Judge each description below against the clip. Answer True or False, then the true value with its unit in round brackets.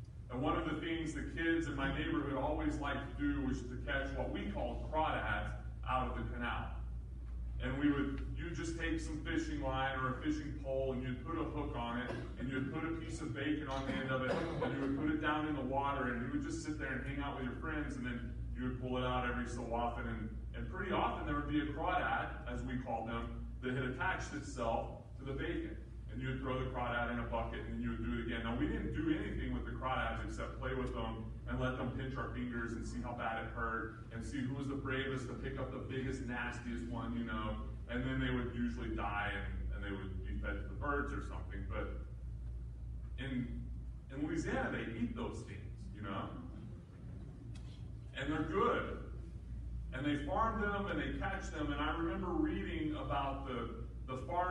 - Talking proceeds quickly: True (230 wpm)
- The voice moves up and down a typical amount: True (3.5 semitones)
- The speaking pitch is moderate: False (125 Hz)